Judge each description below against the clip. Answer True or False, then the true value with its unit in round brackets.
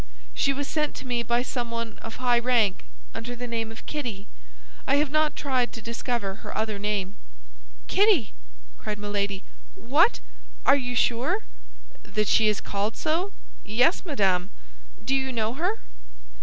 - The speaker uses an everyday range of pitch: True (4.2 semitones)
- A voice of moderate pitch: False (235 Hz)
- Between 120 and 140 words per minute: False (155 wpm)